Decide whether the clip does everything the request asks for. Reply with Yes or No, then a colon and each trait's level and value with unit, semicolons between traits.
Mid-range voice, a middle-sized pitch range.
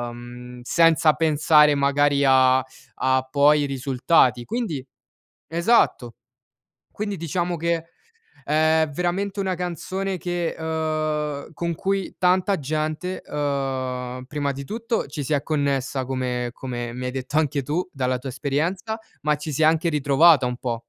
Yes: medium, 150 Hz; average, 4.2 semitones